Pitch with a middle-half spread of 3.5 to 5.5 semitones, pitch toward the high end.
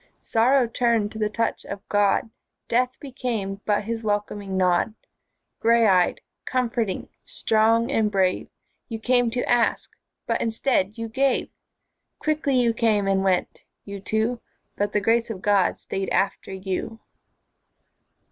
No: average, 2.7 semitones; high, 220 Hz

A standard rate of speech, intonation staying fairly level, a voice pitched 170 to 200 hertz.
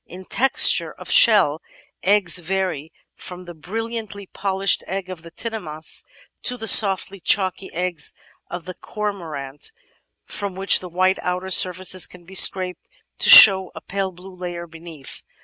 Yes: average, 150 wpm; narrow, 2.1 semitones; medium, 185 Hz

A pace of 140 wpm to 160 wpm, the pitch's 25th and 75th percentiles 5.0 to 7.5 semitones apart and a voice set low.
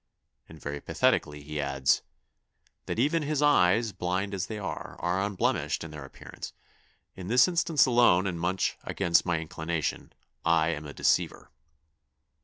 Yes: average, 150 wpm; wide, 5.4 semitones; very low, 90 Hz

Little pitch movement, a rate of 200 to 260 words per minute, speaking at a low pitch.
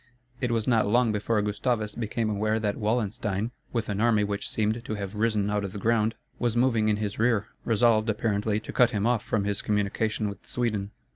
Yes: narrow, 2.0 semitones; fast, 205 wpm; low, 110 Hz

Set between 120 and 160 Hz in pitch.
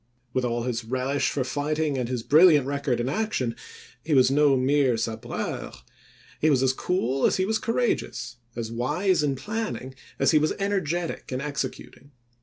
Yes: medium, 140 Hz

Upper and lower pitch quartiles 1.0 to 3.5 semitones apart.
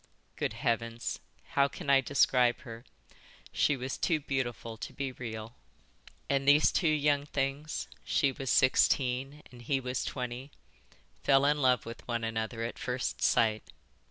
Yes: average, 2.9 semitones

